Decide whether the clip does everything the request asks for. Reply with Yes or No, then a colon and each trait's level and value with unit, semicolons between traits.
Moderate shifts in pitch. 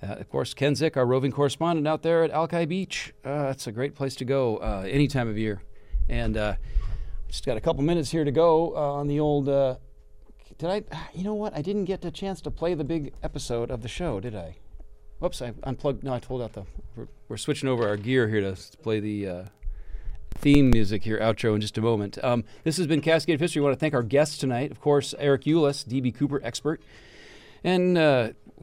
No: wide, 5.7 semitones